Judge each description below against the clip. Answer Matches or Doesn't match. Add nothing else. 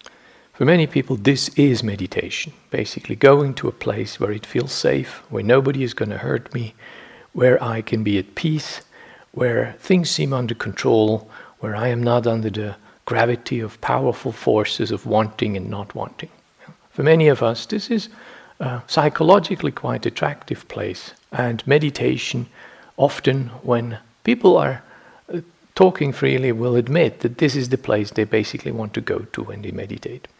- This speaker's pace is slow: Doesn't match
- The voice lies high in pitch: Doesn't match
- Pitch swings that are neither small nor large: Matches